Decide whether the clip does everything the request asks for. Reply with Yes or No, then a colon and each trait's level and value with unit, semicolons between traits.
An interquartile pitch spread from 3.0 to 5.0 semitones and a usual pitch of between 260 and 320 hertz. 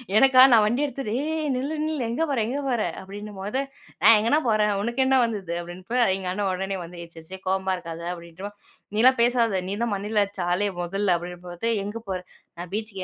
No: average, 4.2 semitones; high, 205 Hz